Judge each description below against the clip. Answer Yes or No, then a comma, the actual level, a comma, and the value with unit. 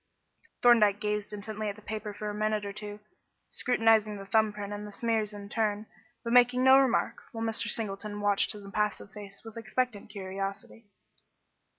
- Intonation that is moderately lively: No, narrow, 1.6 semitones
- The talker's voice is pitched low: No, high, 210 Hz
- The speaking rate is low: No, average, 175 wpm